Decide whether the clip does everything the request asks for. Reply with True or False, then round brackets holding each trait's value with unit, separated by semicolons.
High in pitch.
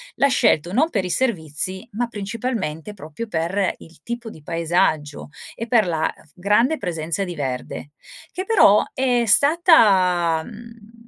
True (200 Hz)